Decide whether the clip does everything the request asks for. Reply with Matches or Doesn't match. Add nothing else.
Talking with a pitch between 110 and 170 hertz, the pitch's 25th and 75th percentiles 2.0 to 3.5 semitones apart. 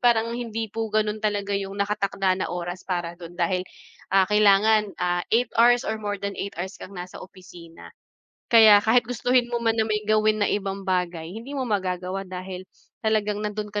Doesn't match